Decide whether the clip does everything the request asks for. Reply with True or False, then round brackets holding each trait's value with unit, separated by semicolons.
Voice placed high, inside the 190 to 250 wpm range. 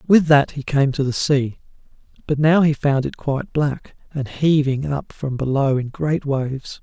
False (140 Hz; 195 wpm)